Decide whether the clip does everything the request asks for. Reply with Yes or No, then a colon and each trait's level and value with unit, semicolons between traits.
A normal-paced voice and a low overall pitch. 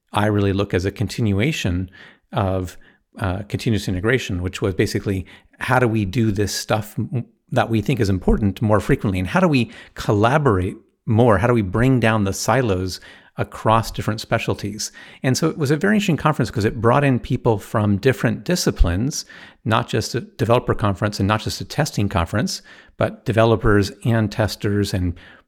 Yes: average, 175 wpm; low, 110 Hz